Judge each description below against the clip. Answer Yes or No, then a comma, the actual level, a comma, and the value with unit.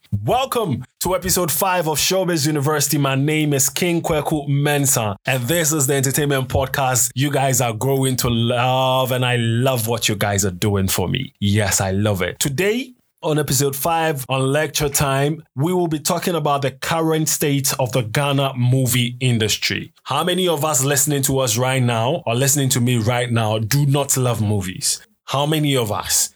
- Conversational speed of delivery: Yes, average, 185 wpm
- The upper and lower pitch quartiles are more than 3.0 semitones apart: Yes, average, 3.9 semitones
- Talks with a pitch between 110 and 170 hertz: Yes, low, 135 Hz